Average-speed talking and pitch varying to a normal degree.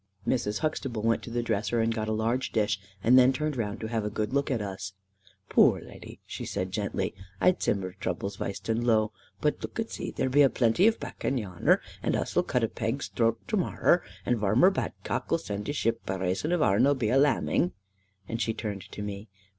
No: fast, 220 wpm; average, 4.0 semitones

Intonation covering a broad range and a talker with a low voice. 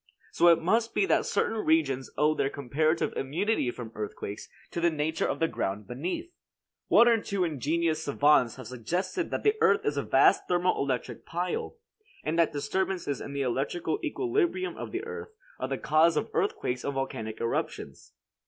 No: wide, 5.9 semitones; medium, 160 Hz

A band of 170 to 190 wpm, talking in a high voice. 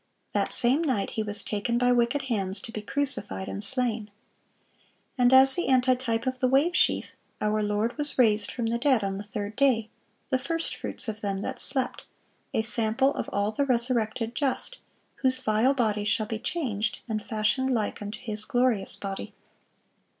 Yes: average, 180 wpm; high, 235 Hz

